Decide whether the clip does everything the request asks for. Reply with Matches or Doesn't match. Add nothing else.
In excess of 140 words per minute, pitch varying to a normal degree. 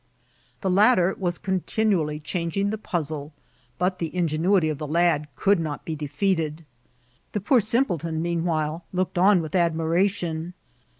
Doesn't match